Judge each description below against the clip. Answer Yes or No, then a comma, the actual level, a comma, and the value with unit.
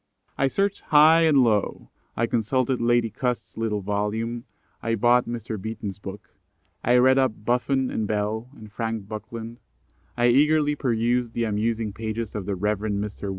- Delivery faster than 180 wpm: No, average, 155 wpm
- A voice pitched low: Yes, low, 115 Hz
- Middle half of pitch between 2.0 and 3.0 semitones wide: Yes, average, 2.7 semitones